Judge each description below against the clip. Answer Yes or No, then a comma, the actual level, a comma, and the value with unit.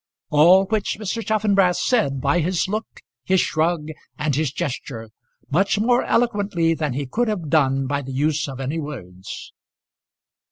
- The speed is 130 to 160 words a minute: Yes, average, 155 wpm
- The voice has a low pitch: No, medium, 160 Hz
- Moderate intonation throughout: No, wide, 6.0 semitones